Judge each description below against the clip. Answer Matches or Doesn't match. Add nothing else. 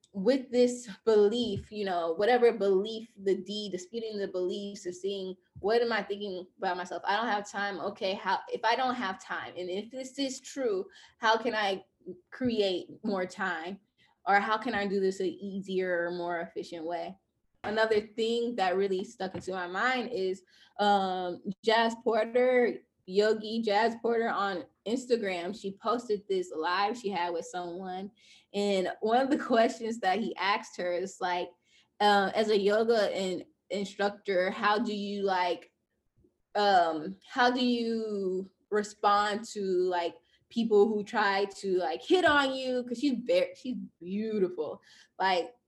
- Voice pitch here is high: Matches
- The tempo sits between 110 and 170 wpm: Matches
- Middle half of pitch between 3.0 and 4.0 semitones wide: Matches